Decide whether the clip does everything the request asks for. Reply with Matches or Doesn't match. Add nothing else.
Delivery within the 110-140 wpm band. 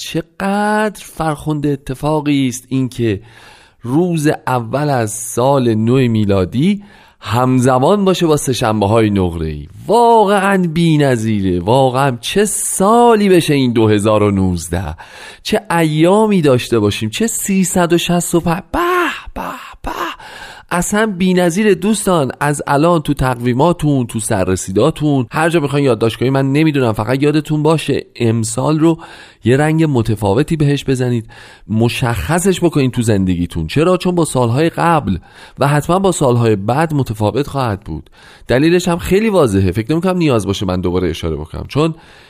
Matches